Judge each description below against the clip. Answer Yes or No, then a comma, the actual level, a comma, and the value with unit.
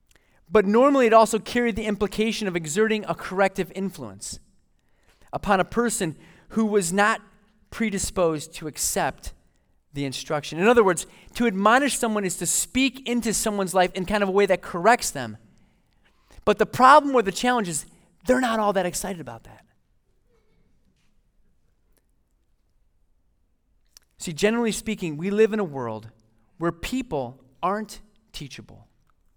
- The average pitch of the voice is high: Yes, high, 195 Hz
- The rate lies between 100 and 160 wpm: Yes, average, 140 wpm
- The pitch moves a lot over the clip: Yes, wide, 6.8 semitones